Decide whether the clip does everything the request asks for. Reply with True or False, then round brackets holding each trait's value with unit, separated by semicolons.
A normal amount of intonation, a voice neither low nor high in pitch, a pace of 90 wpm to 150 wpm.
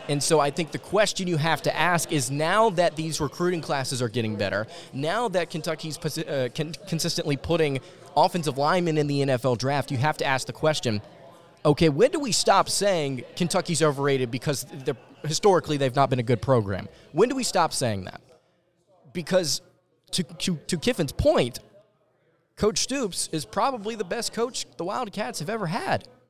False (4.2 semitones; 160 Hz; 175 wpm)